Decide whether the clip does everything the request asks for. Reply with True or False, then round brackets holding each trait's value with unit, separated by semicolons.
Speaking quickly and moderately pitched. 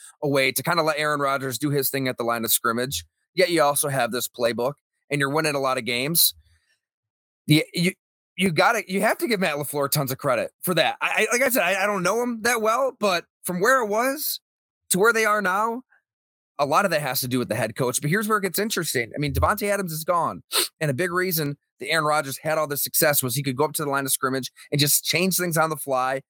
True (265 wpm; 150 Hz)